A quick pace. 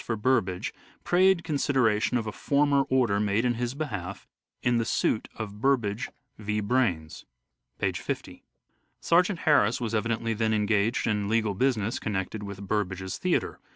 No: average, 155 wpm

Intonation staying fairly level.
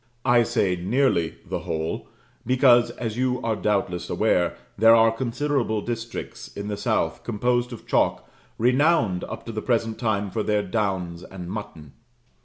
No: average, 3.5 semitones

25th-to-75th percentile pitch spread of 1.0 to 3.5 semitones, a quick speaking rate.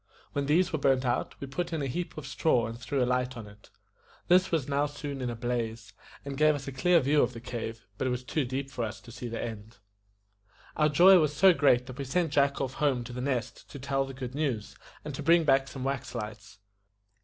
Yes: average, 3.2 semitones; fast, 245 wpm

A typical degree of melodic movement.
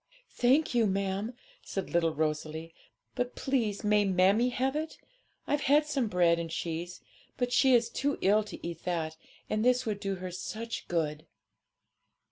No: wide, 6.4 semitones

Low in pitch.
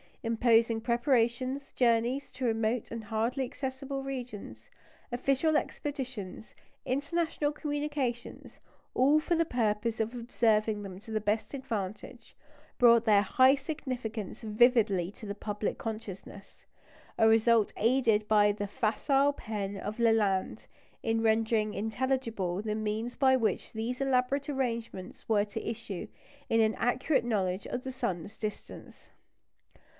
No: high, 230 Hz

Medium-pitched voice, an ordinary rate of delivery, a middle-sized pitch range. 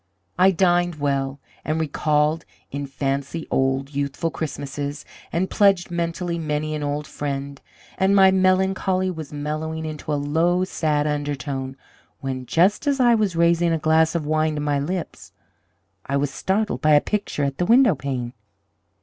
Yes: medium, 155 Hz; average, 155 wpm; average, 3.6 semitones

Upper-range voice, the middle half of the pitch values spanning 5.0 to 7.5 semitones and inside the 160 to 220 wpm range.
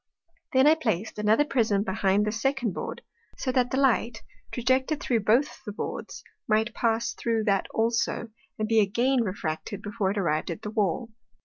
No: high, 225 Hz; average, 3.2 semitones; average, 175 wpm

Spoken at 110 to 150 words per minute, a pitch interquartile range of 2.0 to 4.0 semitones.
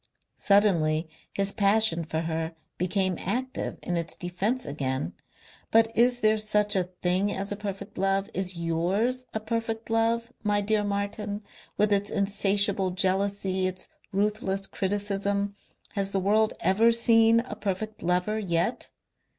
Yes: average, 140 wpm; narrow, 2.6 semitones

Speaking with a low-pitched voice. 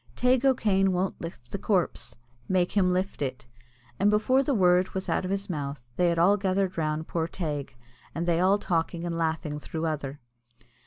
No: medium, 180 Hz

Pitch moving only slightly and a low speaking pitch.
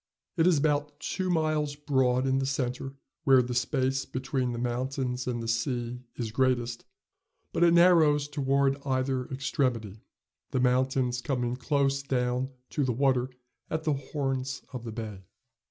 Yes: narrow, 2.3 semitones; low, 130 Hz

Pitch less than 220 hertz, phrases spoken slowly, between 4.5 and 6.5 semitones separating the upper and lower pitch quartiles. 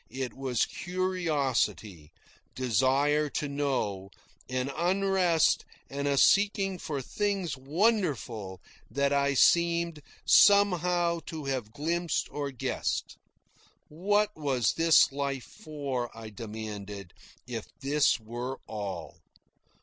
Yes: medium, 140 Hz; slow, 105 wpm; wide, 5.6 semitones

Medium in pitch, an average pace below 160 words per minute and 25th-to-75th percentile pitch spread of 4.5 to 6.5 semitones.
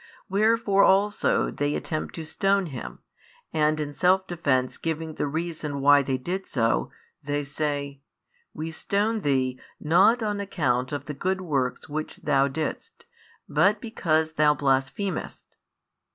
Yes: medium, 155 Hz; average, 140 wpm; average, 5.2 semitones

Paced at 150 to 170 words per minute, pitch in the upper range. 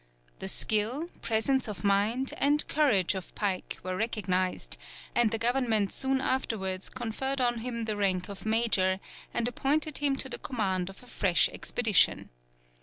Yes: average, 155 wpm; high, 225 Hz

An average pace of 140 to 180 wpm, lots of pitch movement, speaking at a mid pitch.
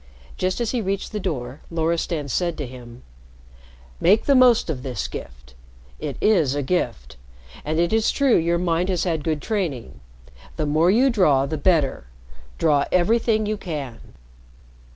Yes: average, 160 wpm; wide, 6.1 semitones; medium, 165 Hz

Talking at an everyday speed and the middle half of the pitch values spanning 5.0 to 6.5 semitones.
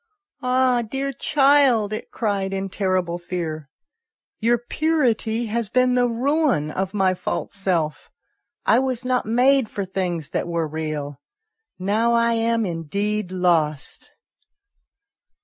No: slow, 130 wpm; wide, 5.6 semitones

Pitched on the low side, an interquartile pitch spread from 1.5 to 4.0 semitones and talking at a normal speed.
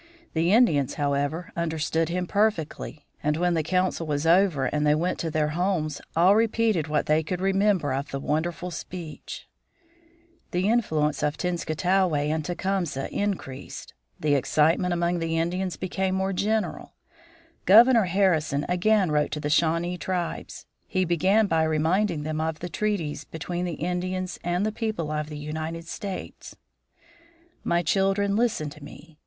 No: medium, 170 Hz; average, 3.6 semitones; average, 150 wpm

